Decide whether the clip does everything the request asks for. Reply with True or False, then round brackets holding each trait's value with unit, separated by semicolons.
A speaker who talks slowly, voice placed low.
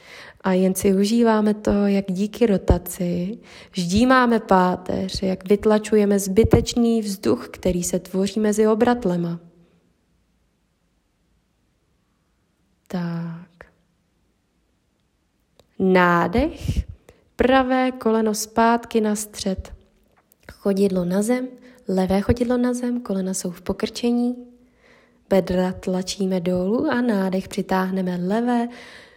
False (95 wpm; 205 Hz)